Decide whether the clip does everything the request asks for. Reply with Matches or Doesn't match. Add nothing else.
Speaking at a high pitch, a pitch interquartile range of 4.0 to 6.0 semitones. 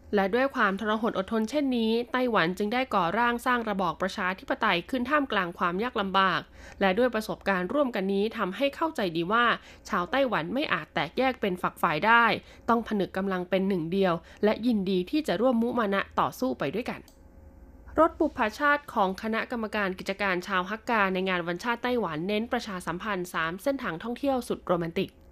Matches